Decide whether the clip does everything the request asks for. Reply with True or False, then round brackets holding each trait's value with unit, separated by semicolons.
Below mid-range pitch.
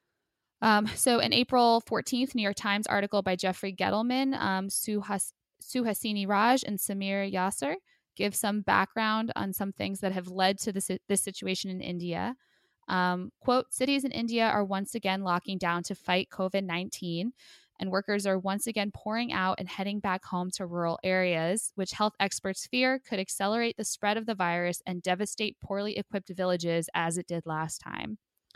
False (195 Hz)